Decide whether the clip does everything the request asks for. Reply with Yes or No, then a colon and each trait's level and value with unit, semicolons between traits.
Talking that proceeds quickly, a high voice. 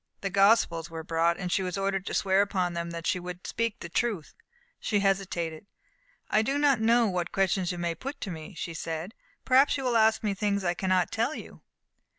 Yes: fast, 210 wpm; high, 195 Hz